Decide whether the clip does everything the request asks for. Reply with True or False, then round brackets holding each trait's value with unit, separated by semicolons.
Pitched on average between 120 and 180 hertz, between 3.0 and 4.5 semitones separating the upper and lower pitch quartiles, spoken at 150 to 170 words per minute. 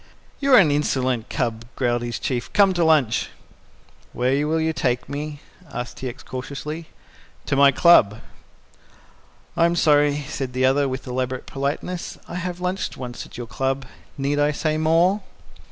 True (140 Hz; 3.9 semitones; 160 wpm)